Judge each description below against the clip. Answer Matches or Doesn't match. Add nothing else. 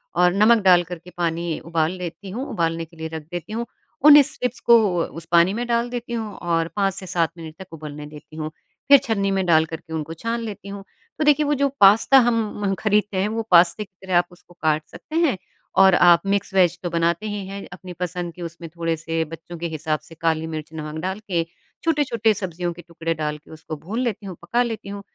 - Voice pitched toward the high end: Doesn't match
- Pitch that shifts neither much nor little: Matches